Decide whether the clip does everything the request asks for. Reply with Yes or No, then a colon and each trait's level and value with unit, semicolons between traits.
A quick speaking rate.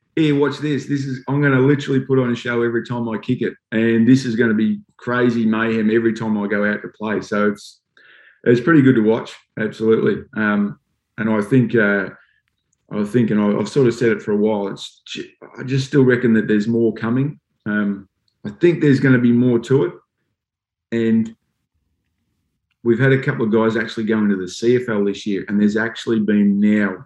Yes: fast, 210 wpm